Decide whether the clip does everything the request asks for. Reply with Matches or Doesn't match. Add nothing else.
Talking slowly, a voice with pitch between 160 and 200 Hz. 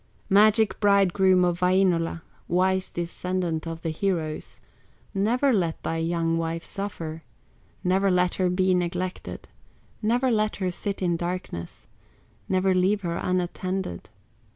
Matches